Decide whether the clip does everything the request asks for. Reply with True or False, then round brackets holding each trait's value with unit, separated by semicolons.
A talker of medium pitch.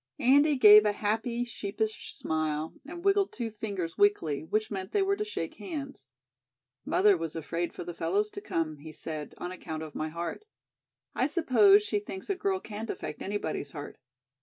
False (215 Hz)